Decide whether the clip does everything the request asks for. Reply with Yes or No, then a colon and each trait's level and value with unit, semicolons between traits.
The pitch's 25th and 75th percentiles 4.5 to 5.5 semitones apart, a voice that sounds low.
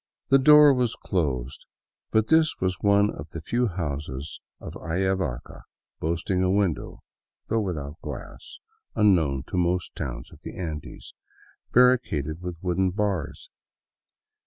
Yes: average, 5.2 semitones; very low, 90 Hz